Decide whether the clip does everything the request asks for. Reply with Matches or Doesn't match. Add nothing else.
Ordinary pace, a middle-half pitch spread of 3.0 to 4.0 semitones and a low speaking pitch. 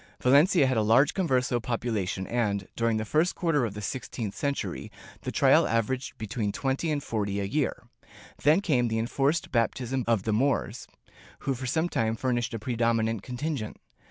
Matches